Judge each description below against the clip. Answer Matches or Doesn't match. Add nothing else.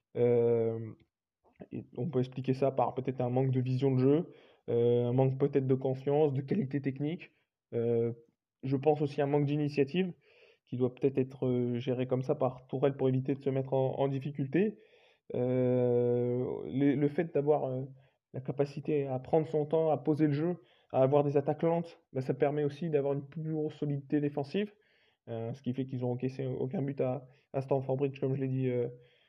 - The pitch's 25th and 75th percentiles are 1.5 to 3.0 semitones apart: Matches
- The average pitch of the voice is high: Doesn't match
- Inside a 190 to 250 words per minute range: Matches